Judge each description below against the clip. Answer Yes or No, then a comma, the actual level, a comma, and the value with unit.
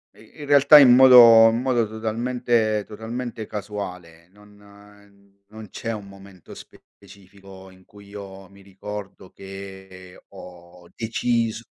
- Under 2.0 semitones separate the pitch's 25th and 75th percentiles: No, average, 2.7 semitones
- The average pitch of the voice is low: Yes, low, 105 Hz